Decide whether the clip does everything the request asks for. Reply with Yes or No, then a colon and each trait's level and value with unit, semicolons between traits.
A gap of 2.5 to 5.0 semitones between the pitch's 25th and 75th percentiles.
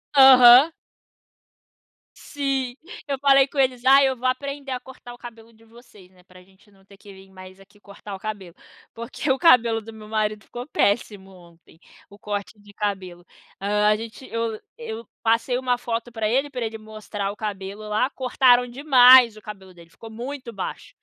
Yes: average, 3.8 semitones